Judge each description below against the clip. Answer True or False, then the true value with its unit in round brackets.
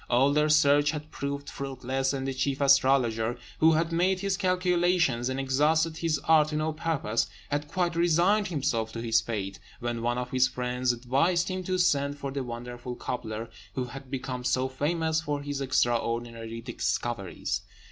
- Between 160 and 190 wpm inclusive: True (170 wpm)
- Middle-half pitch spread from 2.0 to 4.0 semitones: False (4.5 semitones)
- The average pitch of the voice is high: False (135 Hz)